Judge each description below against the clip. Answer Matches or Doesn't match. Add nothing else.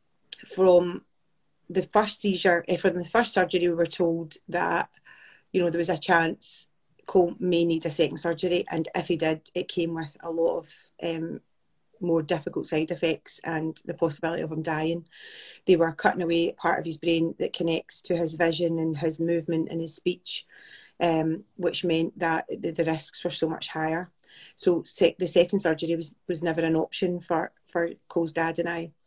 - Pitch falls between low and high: Matches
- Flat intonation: Matches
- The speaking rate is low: Doesn't match